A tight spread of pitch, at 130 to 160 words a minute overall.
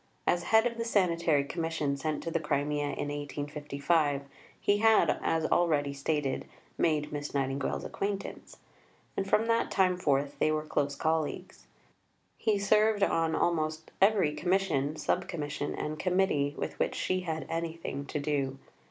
No: average, 4.0 semitones; average, 150 wpm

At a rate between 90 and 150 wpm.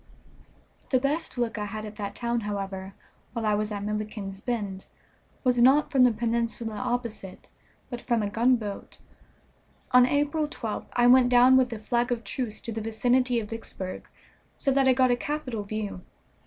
No: average, 175 wpm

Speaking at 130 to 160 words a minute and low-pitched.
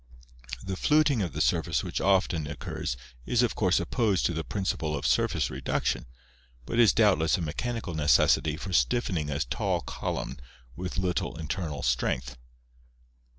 Yes: average, 150 wpm; very low, 90 Hz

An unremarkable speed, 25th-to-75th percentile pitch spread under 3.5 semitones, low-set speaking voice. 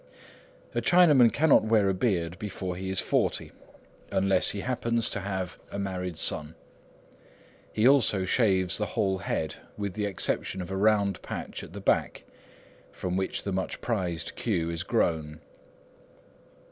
Yes: average, 150 wpm; average, 2.9 semitones; very low, 95 Hz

